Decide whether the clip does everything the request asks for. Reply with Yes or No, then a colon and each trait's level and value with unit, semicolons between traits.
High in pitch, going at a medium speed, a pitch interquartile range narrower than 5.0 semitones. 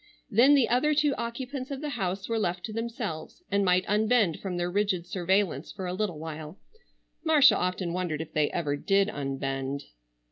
No: high, 195 Hz; average, 180 wpm; wide, 5.6 semitones